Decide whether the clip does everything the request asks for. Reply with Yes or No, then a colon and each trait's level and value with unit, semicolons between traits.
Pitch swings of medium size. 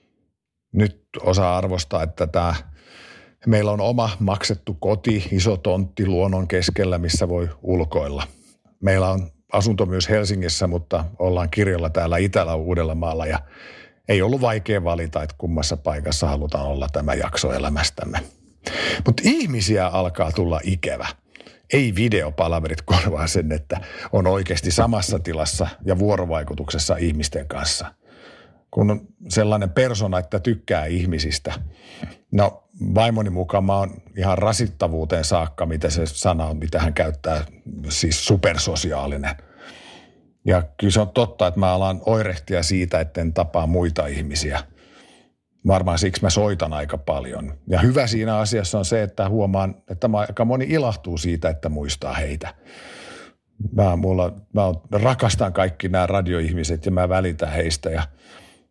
Yes: average, 3.9 semitones